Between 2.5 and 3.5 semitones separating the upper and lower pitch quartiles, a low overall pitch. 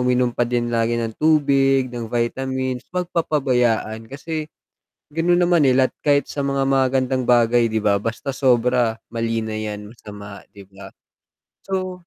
Yes: average, 3.2 semitones; low, 125 Hz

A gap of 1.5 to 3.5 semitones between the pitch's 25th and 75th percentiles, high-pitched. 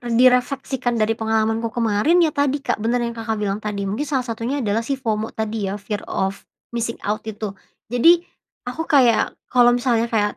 Yes: average, 2.7 semitones; high, 230 Hz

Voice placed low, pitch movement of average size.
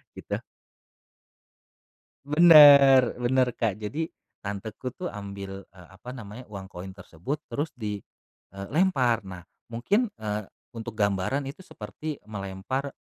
No: low, 115 Hz; wide, 6.2 semitones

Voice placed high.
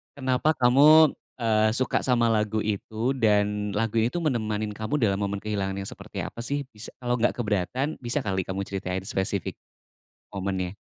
No: low, 110 Hz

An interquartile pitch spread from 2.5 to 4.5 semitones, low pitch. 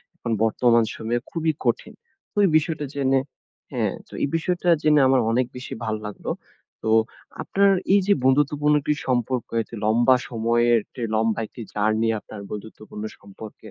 No: average, 4.9 semitones; low, 120 Hz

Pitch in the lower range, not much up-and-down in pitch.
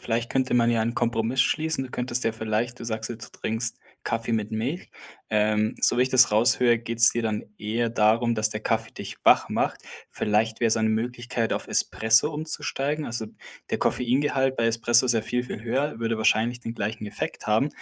Yes: low, 115 Hz; narrow, 1.9 semitones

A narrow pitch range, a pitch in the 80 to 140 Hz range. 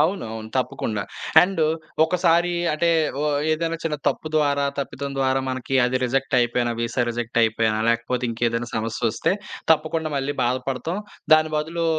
No: average, 4.9 semitones; low, 135 Hz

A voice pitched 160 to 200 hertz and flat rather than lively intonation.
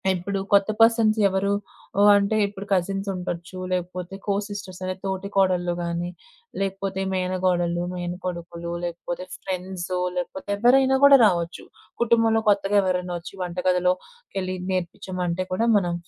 Yes: medium, 185 Hz; narrow, 2.0 semitones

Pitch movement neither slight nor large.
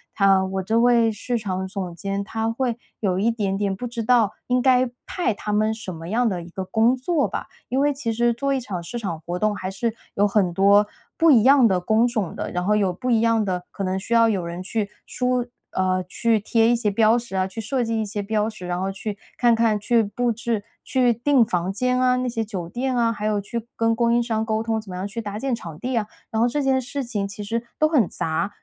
Yes: average, 3.4 semitones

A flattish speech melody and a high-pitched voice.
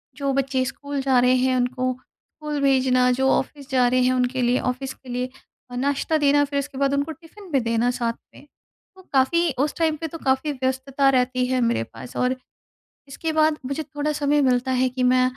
Yes: narrow, 2.2 semitones; very high, 265 Hz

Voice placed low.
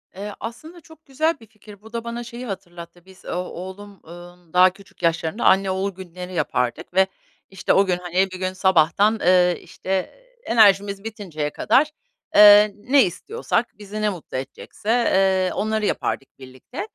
No: high, 195 Hz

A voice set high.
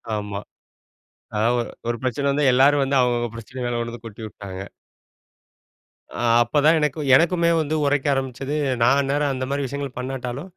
No: low, 130 Hz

